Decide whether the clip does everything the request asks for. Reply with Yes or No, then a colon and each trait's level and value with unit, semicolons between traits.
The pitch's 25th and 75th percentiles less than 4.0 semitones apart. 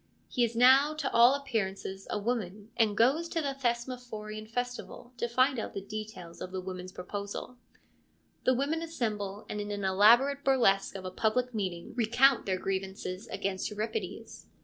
No: average, 4.3 semitones